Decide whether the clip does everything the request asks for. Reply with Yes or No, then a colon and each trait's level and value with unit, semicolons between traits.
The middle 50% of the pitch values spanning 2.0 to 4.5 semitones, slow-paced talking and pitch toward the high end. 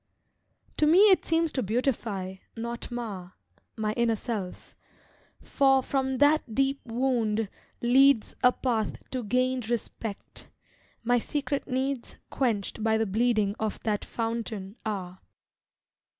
Yes: average, 3.7 semitones; slow, 120 wpm; high, 235 Hz